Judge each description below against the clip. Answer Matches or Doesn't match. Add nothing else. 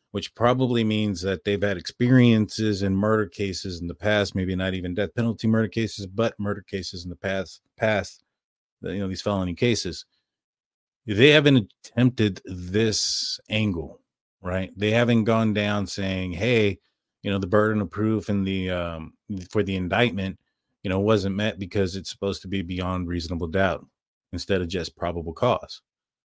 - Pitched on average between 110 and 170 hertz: Doesn't match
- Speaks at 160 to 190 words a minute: Matches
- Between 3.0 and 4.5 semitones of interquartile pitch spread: Doesn't match